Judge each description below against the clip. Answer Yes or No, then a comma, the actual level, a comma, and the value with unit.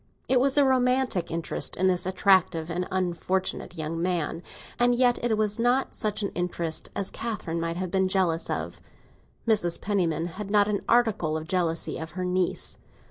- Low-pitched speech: No, medium, 185 Hz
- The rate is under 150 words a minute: No, average, 175 wpm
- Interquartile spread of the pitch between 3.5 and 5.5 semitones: Yes, average, 4.2 semitones